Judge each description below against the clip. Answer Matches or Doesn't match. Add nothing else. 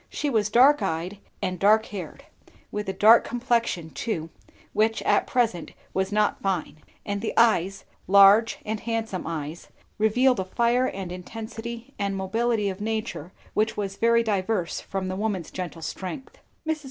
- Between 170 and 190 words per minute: Doesn't match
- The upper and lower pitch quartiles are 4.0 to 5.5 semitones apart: Doesn't match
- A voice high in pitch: Matches